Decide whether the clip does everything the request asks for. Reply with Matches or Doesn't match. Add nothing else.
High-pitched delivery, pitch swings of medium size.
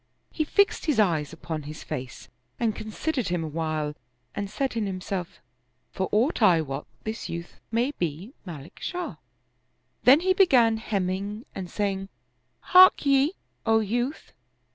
Doesn't match